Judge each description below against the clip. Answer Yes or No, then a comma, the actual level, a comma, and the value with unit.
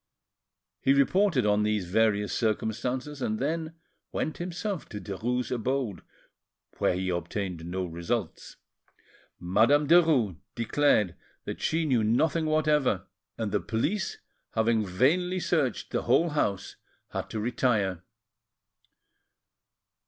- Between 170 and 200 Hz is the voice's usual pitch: No, low, 115 Hz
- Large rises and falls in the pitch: Yes, wide, 6.4 semitones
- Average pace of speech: No, slow, 115 wpm